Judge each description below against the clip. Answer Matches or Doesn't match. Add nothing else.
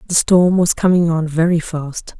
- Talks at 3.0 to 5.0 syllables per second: Matches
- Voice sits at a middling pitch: Matches